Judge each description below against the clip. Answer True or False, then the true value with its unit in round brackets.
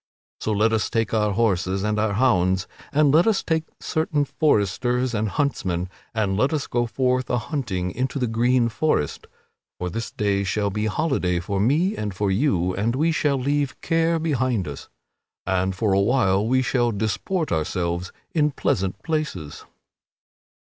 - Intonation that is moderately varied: False (6.1 semitones)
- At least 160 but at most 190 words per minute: True (165 wpm)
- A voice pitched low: True (115 Hz)